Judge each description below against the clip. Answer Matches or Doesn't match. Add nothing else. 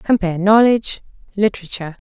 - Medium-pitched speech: Doesn't match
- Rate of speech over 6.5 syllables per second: Matches